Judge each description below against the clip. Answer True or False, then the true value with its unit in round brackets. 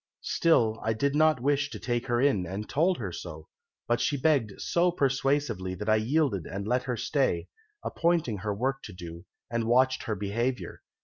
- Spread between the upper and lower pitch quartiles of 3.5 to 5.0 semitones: False (5.4 semitones)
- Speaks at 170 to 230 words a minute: True (185 wpm)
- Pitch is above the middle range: False (120 Hz)